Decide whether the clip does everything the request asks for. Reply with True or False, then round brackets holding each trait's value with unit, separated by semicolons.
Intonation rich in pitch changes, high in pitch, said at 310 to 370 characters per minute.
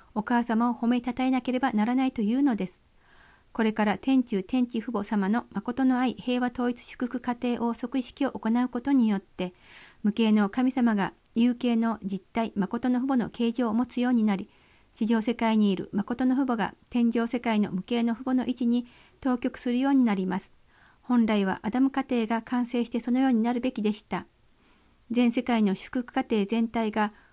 False (2.5 semitones; 240 Hz; 355 characters per minute)